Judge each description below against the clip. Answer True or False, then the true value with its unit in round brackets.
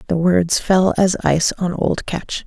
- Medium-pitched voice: True (180 Hz)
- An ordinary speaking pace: True (195 wpm)